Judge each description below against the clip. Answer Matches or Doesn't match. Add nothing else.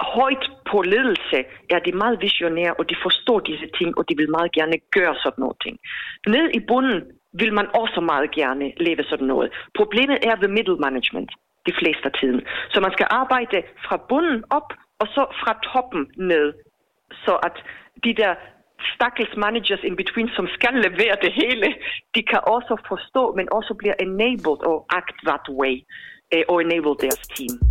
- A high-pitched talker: Matches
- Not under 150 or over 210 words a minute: Matches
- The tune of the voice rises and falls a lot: Matches